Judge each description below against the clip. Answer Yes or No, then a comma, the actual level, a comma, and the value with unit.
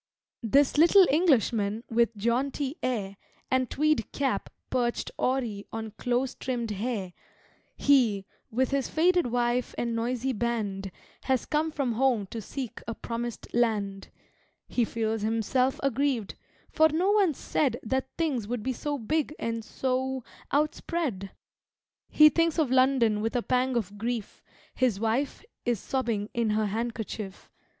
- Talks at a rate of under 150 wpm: Yes, average, 140 wpm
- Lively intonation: No, average, 3.4 semitones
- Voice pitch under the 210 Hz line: No, high, 240 Hz